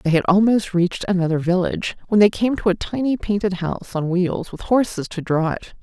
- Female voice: Yes, female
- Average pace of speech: No, fast, 215 wpm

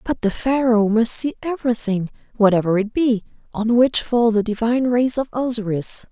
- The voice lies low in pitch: No, high, 230 Hz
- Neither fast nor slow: Yes, average, 165 wpm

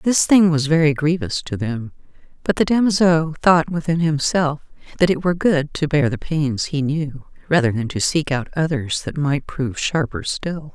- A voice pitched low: No, medium, 150 Hz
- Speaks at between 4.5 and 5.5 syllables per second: Yes, 4.7 syllables/s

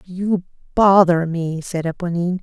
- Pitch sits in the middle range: Yes, medium, 175 Hz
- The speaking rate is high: No, slow, 125 wpm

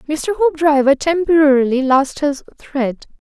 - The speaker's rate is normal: No, slow, 110 wpm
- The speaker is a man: No, female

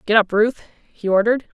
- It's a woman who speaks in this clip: Yes, female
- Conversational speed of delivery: Yes, average, 190 wpm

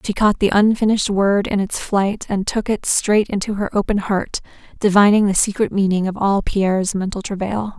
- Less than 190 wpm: No, average, 195 wpm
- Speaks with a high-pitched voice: Yes, high, 200 Hz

